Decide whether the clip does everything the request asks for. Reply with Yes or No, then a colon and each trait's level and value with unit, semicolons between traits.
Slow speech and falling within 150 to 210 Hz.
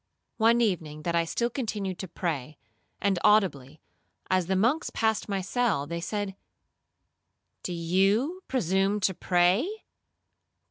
Yes: slow, 130 wpm; high, 190 Hz